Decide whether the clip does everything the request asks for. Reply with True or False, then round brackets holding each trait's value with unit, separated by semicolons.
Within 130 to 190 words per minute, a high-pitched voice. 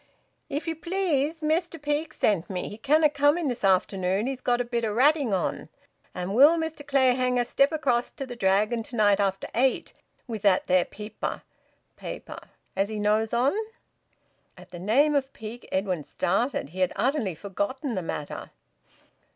True (170 wpm; 240 Hz)